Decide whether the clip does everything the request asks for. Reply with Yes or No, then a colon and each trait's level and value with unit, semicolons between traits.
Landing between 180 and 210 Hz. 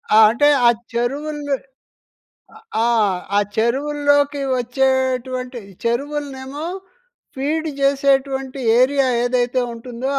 No: very high, 265 Hz